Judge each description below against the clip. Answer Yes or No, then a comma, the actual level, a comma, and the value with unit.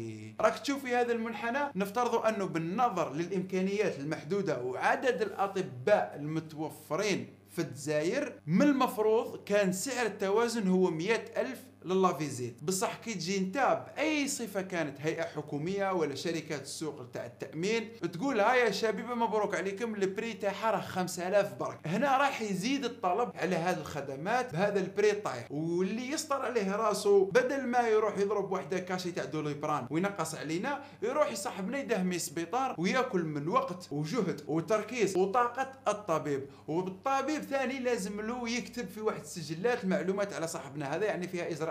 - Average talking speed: No, fast, 140 wpm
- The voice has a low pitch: No, high, 200 Hz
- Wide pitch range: Yes, wide, 5.8 semitones